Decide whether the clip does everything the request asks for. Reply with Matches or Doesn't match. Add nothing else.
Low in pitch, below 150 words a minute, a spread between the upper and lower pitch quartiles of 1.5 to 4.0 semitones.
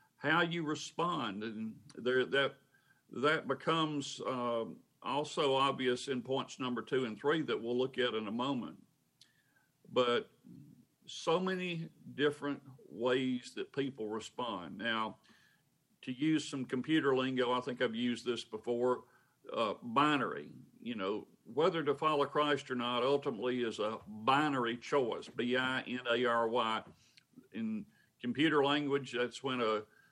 Matches